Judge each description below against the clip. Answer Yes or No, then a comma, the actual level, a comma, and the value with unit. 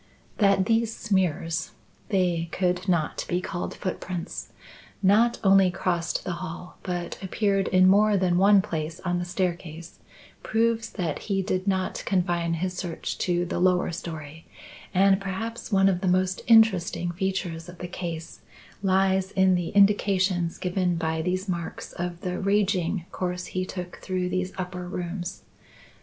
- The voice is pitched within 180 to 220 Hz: Yes, medium, 185 Hz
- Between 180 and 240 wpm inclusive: No, average, 150 wpm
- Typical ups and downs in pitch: No, narrow, 1.7 semitones